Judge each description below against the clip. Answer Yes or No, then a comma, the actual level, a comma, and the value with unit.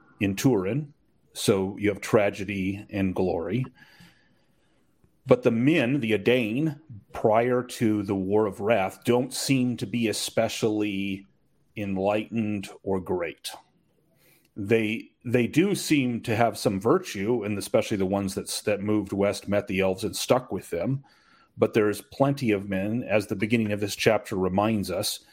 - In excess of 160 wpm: No, average, 150 wpm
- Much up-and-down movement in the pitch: No, average, 3.2 semitones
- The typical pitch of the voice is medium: No, low, 105 Hz